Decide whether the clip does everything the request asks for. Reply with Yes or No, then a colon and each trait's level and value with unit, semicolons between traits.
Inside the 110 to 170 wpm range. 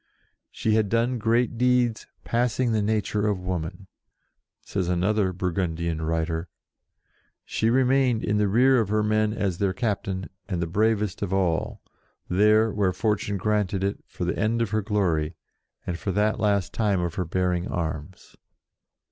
Yes: average, 155 wpm